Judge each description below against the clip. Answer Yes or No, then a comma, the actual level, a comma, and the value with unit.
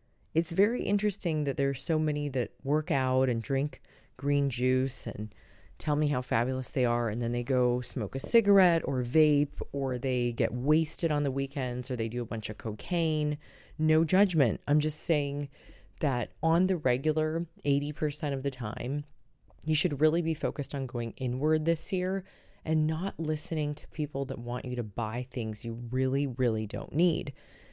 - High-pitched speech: No, medium, 140 Hz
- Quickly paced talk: No, average, 180 wpm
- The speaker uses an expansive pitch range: No, average, 4.1 semitones